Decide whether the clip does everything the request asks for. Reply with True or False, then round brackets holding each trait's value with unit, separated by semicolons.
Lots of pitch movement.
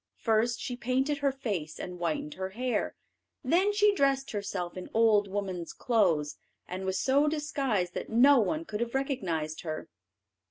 True (6.8 semitones)